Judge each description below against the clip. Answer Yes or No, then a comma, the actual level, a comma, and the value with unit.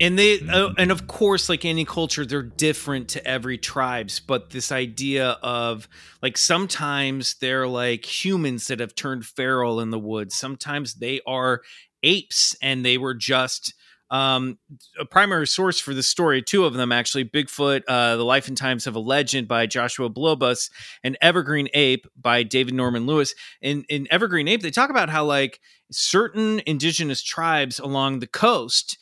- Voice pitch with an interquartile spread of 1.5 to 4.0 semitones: Yes, average, 3.7 semitones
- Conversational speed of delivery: Yes, average, 170 wpm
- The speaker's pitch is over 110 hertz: Yes, low, 135 Hz